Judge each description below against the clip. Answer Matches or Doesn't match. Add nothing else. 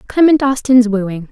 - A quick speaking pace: Doesn't match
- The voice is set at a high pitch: Matches